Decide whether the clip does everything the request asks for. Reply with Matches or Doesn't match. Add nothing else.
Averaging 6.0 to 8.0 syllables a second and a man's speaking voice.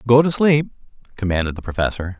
Matches